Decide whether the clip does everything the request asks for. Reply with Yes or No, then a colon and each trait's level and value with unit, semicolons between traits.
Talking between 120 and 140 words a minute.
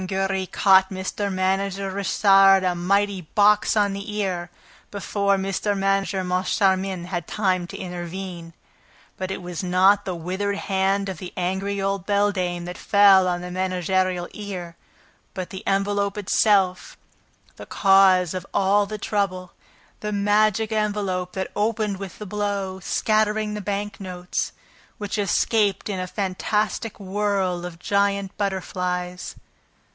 Yes: slow, 135 wpm